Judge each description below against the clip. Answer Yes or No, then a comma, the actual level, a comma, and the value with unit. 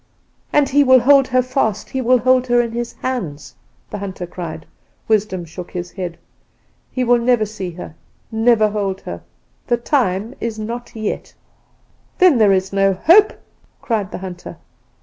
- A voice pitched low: No, high, 220 Hz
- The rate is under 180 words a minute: Yes, average, 165 wpm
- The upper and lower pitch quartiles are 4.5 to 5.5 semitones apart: Yes, average, 4.8 semitones